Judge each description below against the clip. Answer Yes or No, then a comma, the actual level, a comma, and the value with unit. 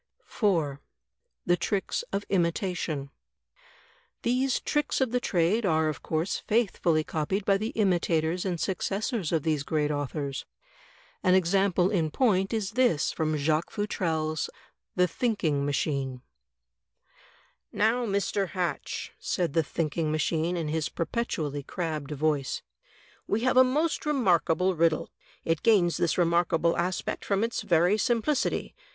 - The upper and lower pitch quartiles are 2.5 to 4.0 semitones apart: No, average, 4.6 semitones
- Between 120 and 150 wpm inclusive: Yes, slow, 135 wpm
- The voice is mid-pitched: Yes, medium, 175 Hz